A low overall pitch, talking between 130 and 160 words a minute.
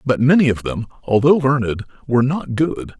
No: low, 130 Hz; average, 180 wpm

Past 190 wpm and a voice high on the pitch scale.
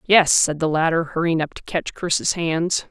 No: fast, 205 wpm; medium, 165 Hz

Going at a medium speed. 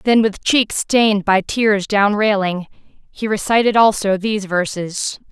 Yes: average, 145 wpm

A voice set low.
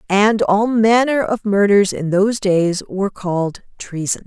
No: high, 200 Hz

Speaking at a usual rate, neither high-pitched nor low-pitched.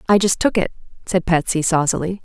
Yes: average, 190 wpm; medium, 180 Hz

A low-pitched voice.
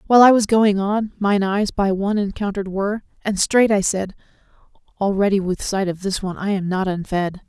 No: high, 200 Hz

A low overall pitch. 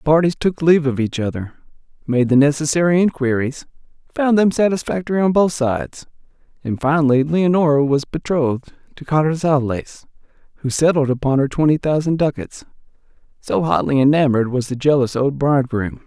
No: medium, 145 Hz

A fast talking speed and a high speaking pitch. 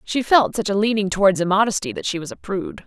Yes: fast, 250 wpm; high, 205 Hz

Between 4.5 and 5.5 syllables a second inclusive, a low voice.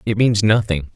Yes: 4.9 syllables/s; low, 105 Hz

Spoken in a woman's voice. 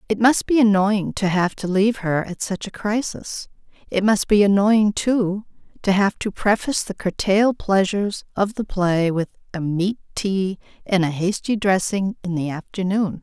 Yes: female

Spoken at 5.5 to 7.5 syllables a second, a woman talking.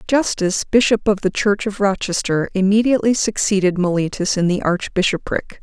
No: 5.1 syllables/s; female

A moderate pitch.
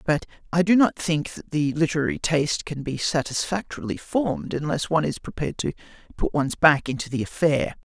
Yes: medium, 150 Hz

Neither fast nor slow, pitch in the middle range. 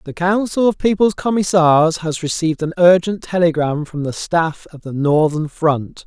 Yes: average, 170 wpm; medium, 165 Hz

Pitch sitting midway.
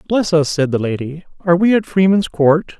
Yes: medium, 170 Hz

